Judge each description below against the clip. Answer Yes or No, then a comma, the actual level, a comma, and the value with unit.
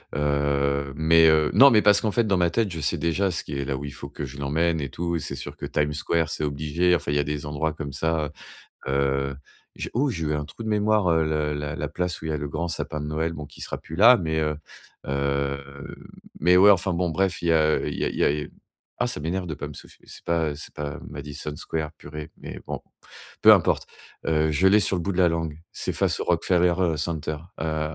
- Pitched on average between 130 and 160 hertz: No, very low, 80 Hz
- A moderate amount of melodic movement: Yes, average, 3.0 semitones